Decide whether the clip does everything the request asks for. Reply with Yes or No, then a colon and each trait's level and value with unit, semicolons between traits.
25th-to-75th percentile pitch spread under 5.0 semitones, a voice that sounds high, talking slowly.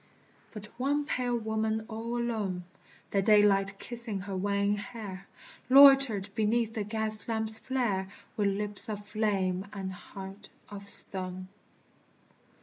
Yes: narrow, 2.4 semitones; high, 210 Hz; slow, 125 wpm